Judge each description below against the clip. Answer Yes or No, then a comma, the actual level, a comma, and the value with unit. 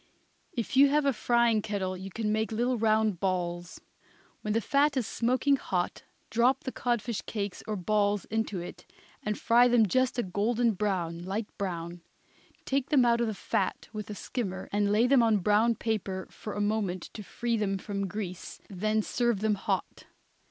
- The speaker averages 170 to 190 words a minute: Yes, average, 180 wpm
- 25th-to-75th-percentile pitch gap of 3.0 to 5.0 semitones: Yes, average, 3.4 semitones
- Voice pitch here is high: Yes, high, 215 Hz